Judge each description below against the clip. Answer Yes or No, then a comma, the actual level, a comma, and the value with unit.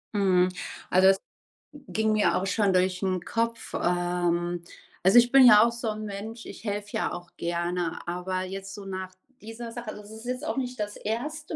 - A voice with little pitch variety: No, average, 3.9 semitones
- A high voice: Yes, high, 205 Hz